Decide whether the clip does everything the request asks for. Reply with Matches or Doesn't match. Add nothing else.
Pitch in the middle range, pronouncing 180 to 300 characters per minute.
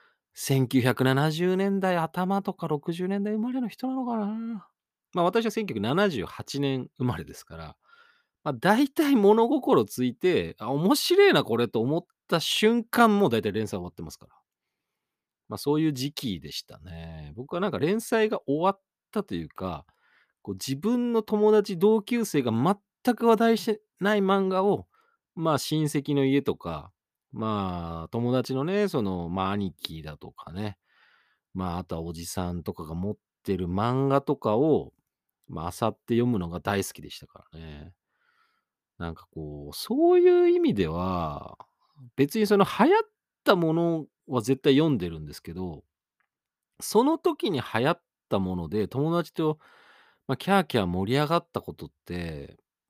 Matches